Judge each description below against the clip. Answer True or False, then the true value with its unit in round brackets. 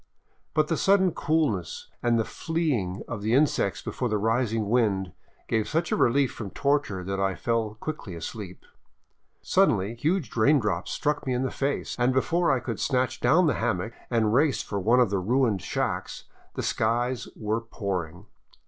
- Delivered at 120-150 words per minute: False (170 wpm)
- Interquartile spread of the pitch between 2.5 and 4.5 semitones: False (5.3 semitones)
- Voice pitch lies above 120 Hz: False (115 Hz)